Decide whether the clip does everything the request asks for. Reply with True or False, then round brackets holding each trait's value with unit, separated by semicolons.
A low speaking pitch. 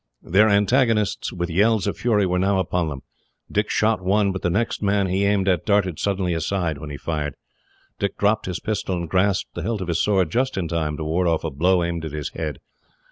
True (95 Hz)